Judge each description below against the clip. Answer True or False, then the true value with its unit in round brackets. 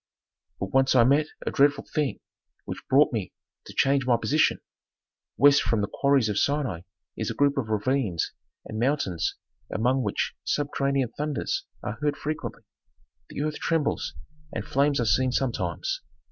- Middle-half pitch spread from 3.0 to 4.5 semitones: True (3.9 semitones)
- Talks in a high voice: False (135 Hz)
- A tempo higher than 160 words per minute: False (155 wpm)